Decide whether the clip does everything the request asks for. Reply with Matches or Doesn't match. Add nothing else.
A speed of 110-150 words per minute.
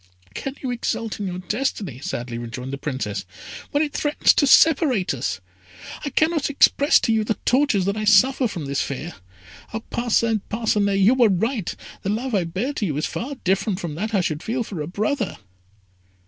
Doesn't match